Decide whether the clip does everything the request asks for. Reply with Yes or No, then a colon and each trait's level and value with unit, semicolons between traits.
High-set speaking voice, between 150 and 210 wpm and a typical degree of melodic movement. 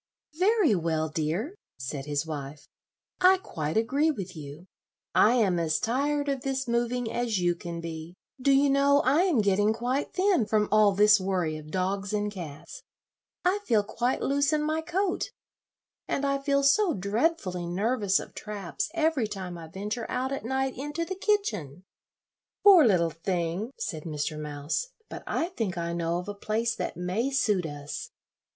No: high, 210 Hz; average, 170 wpm; wide, 8.4 semitones